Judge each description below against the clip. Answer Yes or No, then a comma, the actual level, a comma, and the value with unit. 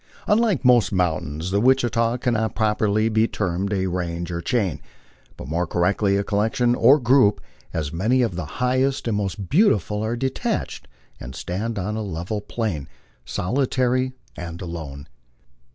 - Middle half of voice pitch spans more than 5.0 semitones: Yes, wide, 5.5 semitones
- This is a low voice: Yes, low, 105 Hz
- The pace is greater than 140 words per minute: Yes, average, 150 wpm